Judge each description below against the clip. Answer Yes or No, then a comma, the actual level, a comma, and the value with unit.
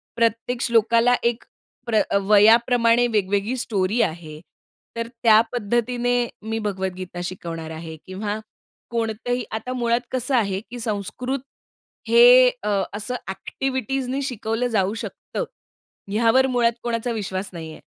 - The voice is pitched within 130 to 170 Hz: No, high, 230 Hz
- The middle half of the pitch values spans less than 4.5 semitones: Yes, average, 3.4 semitones